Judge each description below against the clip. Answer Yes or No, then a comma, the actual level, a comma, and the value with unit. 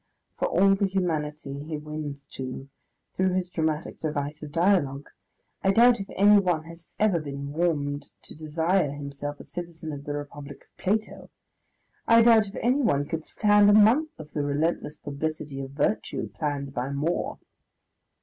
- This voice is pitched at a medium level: Yes, medium, 155 Hz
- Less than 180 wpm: Yes, average, 160 wpm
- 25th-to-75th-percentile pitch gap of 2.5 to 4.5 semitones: No, average, 4.9 semitones